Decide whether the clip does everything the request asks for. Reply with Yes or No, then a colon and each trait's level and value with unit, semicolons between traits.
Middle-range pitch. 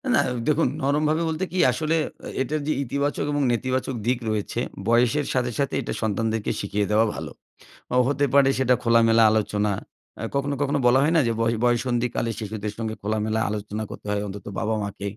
No: low, 120 Hz